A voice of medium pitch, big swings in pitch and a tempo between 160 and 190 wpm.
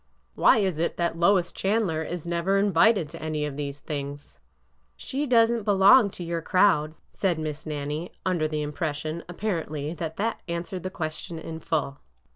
No: medium, 170 Hz; average, 3.8 semitones; average, 180 wpm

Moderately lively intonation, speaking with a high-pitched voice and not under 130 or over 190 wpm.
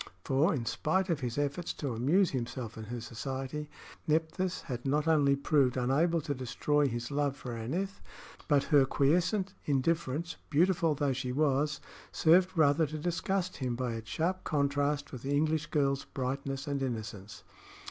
No: average, 3.6 semitones; medium, 145 Hz; average, 160 wpm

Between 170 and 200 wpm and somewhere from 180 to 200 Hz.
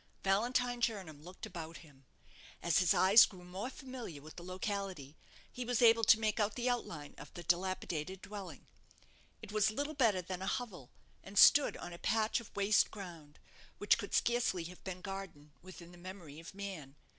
Yes: average, 180 wpm; high, 190 Hz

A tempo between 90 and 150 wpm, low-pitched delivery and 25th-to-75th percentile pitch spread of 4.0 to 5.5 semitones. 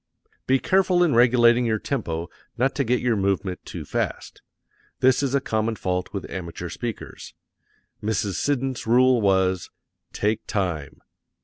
Yes: average, 140 wpm; low, 115 Hz; average, 5.0 semitones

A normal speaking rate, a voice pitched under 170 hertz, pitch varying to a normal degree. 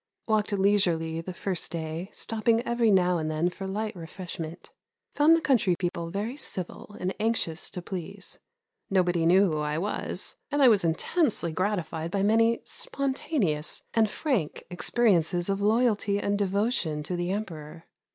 No: average, 150 wpm; high, 190 Hz; average, 4.4 semitones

